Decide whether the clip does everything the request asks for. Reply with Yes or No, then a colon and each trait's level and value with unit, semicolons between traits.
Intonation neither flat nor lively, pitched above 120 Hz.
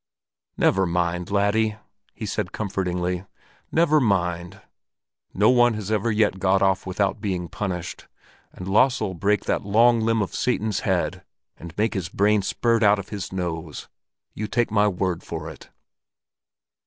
No: average, 3.2 semitones; low, 100 Hz